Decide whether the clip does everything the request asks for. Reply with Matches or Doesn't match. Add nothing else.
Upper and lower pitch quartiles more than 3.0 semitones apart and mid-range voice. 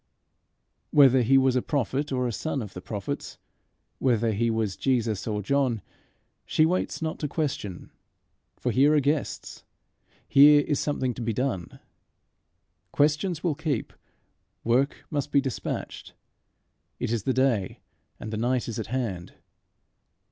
Doesn't match